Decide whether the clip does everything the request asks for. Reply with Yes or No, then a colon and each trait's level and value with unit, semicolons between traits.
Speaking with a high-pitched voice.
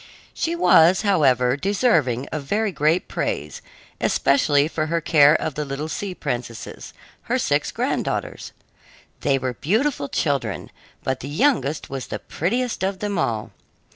No: medium, 155 Hz